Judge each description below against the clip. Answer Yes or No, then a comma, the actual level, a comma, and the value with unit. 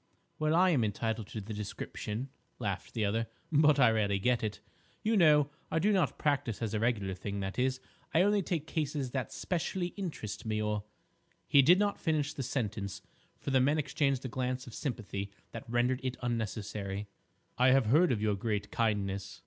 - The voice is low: Yes, low, 125 Hz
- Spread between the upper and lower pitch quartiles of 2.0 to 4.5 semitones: No, wide, 5.6 semitones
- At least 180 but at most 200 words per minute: Yes, average, 190 wpm